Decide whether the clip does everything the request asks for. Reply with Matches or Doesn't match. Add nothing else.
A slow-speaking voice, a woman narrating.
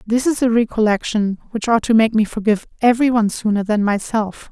Doesn't match